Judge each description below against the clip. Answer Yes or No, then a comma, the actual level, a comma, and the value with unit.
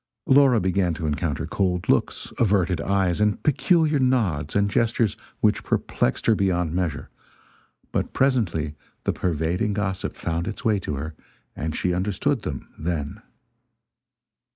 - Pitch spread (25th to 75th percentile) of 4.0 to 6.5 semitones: Yes, average, 5.0 semitones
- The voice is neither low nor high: No, very low, 95 Hz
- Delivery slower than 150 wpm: Yes, slow, 135 wpm